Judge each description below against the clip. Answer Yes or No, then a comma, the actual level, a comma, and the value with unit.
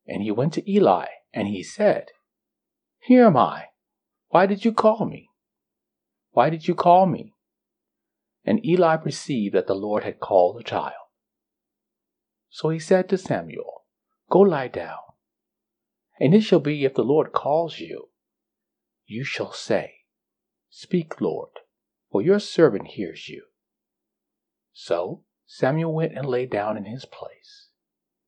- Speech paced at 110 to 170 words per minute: Yes, average, 140 wpm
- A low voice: No, medium, 170 Hz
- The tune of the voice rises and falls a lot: Yes, wide, 6.5 semitones